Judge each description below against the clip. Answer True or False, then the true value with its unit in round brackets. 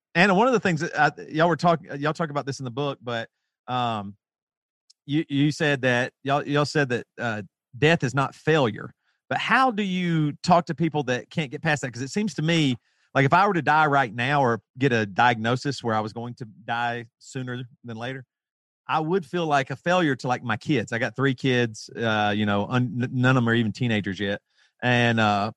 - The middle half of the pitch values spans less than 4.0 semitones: False (4.4 semitones)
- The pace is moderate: False (230 wpm)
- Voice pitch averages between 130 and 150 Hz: True (135 Hz)